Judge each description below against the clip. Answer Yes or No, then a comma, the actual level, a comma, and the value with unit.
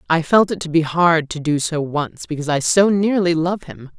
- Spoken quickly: Yes, fast, 240 wpm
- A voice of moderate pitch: Yes, medium, 165 Hz